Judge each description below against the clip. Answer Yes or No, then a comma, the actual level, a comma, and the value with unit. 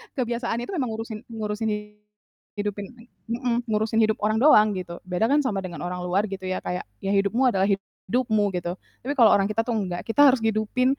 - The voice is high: Yes, high, 215 Hz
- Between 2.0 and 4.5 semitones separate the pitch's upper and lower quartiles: Yes, average, 3.4 semitones